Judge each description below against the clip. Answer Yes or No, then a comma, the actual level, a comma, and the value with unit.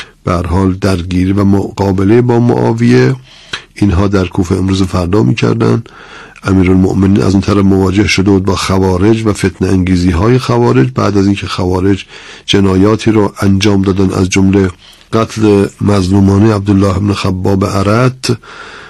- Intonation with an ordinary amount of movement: No, narrow, 1.8 semitones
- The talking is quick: No, average, 135 wpm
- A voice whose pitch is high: No, low, 100 Hz